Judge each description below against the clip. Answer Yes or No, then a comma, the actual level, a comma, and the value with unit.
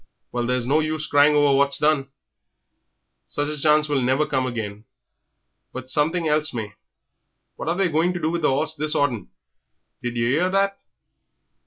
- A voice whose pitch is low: No, medium, 145 Hz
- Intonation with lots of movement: No, average, 3.4 semitones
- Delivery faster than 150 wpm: Yes, average, 170 wpm